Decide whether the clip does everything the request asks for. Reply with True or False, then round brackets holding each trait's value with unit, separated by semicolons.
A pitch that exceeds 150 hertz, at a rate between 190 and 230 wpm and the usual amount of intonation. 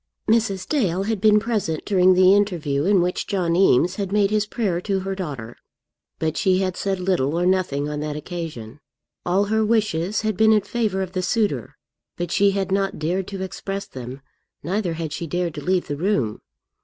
True (185 Hz; 195 wpm; 3.5 semitones)